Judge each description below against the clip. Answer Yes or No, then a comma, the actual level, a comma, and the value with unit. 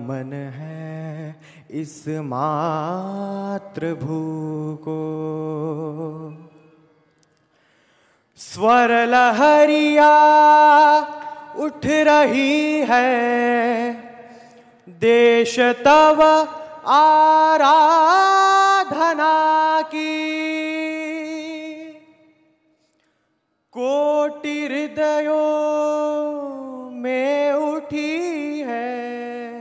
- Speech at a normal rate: No, slow, 35 wpm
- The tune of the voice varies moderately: No, wide, 7.9 semitones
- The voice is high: Yes, very high, 285 Hz